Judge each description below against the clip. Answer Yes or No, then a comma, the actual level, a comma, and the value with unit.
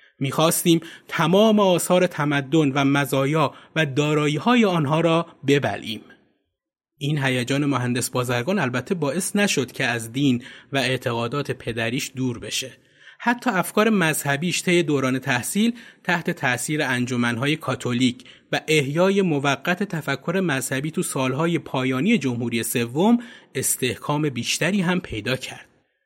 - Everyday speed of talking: Yes, average, 120 wpm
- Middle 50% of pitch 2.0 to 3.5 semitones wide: No, average, 4.9 semitones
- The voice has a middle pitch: Yes, medium, 145 Hz